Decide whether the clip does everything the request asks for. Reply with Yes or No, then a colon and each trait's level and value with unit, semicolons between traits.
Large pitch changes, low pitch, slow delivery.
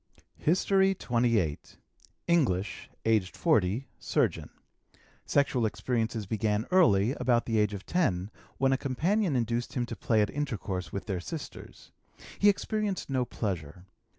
Yes: wide, 6.2 semitones; low, 120 Hz; slow, 130 wpm